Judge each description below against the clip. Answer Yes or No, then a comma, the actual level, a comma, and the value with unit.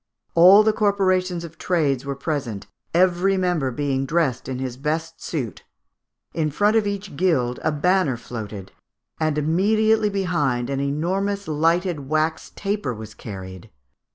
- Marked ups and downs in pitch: Yes, wide, 5.8 semitones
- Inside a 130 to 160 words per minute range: Yes, average, 140 wpm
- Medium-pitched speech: Yes, medium, 160 Hz